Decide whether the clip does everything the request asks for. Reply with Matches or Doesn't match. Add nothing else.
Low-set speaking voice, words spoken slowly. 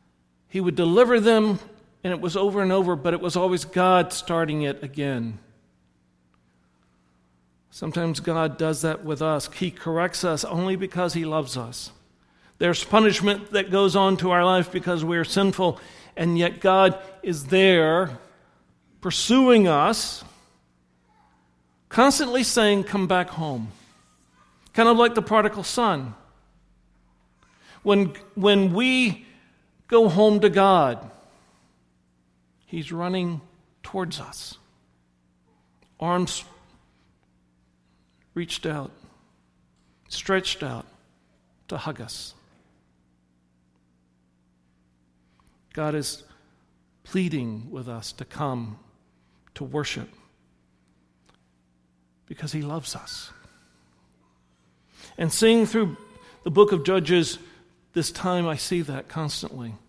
Doesn't match